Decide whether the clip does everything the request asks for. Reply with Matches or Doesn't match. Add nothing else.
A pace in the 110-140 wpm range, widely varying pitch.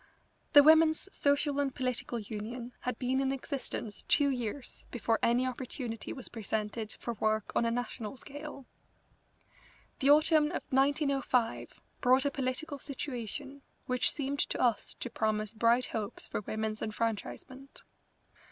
Doesn't match